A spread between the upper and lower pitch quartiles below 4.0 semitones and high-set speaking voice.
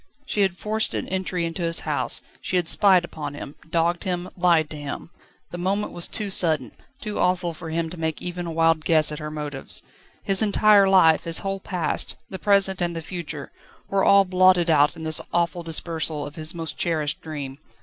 No: average, 2.9 semitones; medium, 170 Hz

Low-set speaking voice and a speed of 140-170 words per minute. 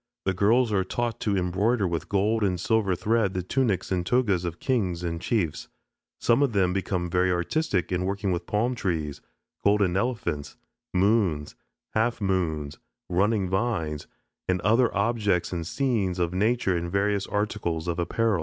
Yes: very low, 95 Hz; average, 155 wpm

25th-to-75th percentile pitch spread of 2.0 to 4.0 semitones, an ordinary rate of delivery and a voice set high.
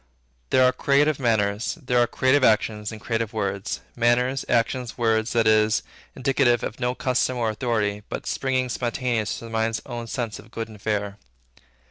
No: narrow, 2.6 semitones; average, 170 wpm; low, 115 Hz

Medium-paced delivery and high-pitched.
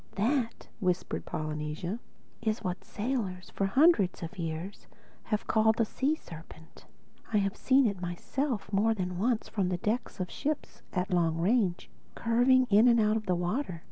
Yes: average, 160 wpm; high, 205 Hz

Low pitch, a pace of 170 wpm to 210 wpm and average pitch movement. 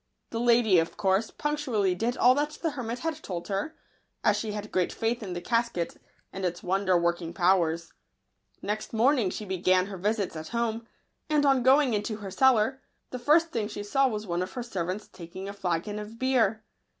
No: high, 210 Hz; average, 195 wpm; average, 4.6 semitones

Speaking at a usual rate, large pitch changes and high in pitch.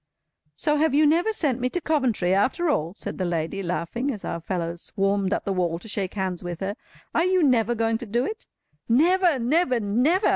No: fast, 210 wpm; wide, 8.0 semitones; high, 230 Hz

